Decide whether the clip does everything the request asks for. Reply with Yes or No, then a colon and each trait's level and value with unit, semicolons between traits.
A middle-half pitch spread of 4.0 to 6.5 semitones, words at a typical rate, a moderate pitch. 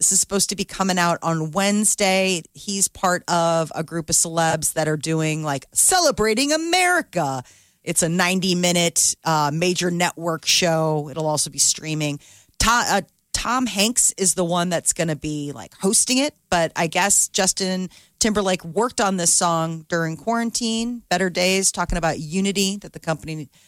No: average, 3.5 semitones; average, 165 wpm; medium, 175 Hz